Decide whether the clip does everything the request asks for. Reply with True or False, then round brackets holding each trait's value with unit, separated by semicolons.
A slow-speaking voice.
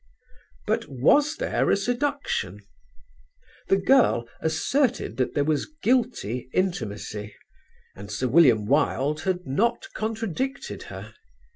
True (110 wpm)